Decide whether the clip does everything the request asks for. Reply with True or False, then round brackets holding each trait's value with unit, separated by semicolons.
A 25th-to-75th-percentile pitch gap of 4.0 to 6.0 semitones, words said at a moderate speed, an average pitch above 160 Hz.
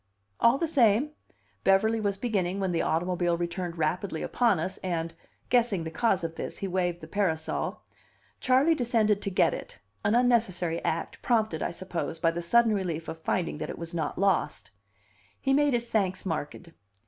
True (5.1 semitones; 175 wpm; 190 Hz)